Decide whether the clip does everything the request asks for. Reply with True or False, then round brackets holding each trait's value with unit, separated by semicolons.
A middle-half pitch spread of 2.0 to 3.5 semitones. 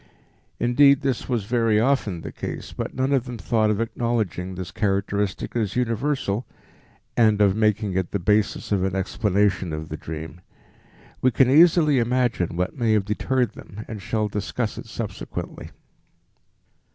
False (4.0 semitones)